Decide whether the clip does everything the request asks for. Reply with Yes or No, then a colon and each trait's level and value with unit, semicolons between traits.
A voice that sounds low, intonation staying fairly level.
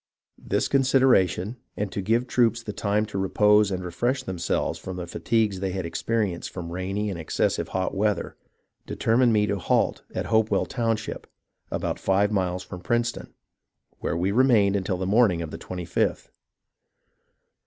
No: low, 100 Hz; average, 3.5 semitones